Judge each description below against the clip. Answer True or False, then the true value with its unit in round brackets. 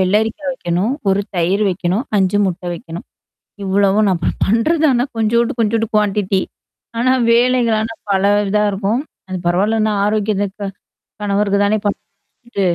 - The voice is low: False (205 Hz)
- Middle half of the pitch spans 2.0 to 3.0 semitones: True (2.7 semitones)